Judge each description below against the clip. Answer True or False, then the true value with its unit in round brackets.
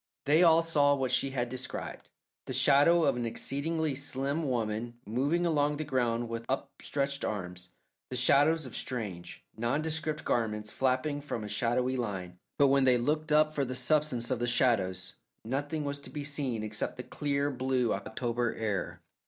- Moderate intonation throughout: True (3.7 semitones)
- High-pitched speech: False (130 Hz)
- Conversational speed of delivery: True (170 wpm)